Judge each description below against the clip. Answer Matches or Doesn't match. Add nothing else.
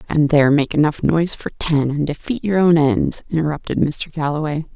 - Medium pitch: Matches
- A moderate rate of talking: Matches